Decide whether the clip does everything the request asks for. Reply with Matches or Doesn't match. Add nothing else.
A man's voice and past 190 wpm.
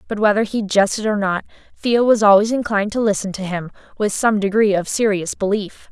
Doesn't match